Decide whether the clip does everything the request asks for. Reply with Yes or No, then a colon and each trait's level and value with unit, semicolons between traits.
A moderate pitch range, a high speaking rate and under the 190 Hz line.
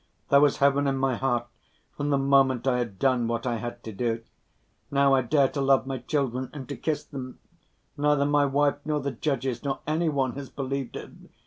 No: narrow, 2.2 semitones; fast, 210 wpm; low, 135 Hz